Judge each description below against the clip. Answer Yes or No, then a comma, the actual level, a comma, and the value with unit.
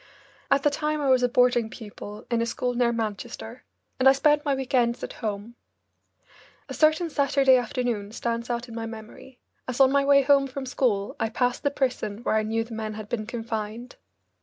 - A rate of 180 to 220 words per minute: Yes, fast, 205 wpm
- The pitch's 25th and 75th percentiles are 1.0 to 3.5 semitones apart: Yes, average, 3.2 semitones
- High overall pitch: Yes, high, 245 Hz